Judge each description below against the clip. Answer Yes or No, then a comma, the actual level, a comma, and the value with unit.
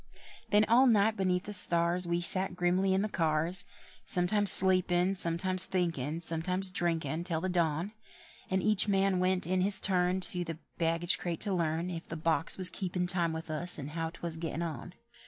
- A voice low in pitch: No, medium, 180 Hz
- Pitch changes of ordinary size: No, narrow, 2.2 semitones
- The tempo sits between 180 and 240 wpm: Yes, average, 185 wpm